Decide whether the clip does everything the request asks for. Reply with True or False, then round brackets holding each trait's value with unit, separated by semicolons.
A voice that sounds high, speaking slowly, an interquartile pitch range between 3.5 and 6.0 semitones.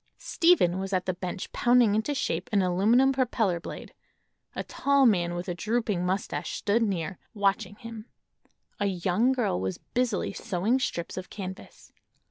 False (200 Hz; 155 wpm; 4.8 semitones)